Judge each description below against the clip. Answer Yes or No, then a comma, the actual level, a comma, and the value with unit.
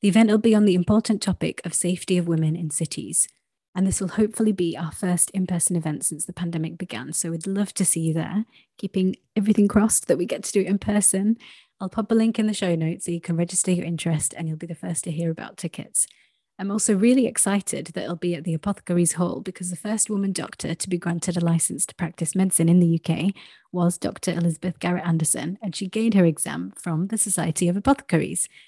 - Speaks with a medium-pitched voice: Yes, medium, 180 Hz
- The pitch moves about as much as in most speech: Yes, average, 3.3 semitones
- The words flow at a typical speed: No, fast, 230 wpm